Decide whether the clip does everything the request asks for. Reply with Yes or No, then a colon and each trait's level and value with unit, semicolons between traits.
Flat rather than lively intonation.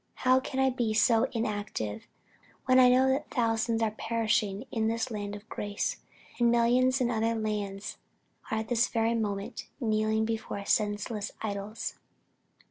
Yes: narrow, 2.2 semitones